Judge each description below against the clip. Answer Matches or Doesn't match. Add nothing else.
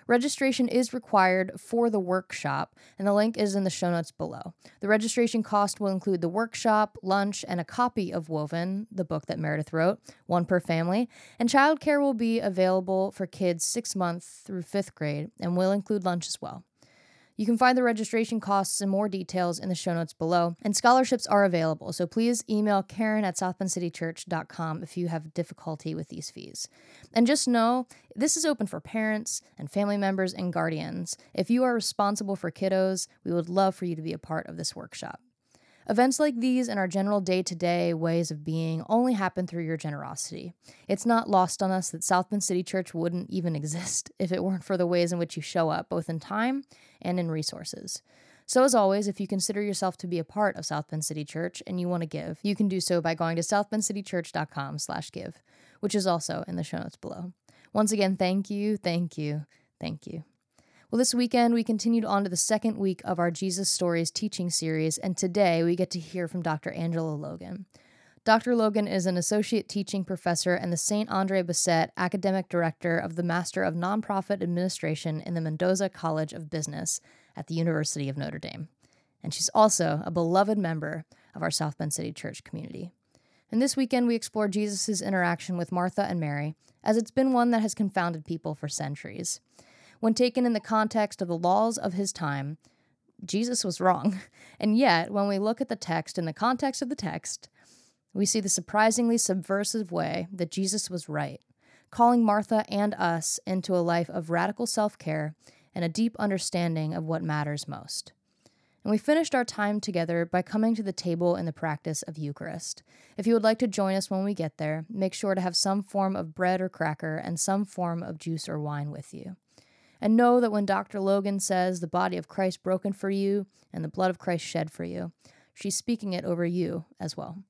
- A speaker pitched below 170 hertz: Doesn't match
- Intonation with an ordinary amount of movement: Matches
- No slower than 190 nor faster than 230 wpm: Matches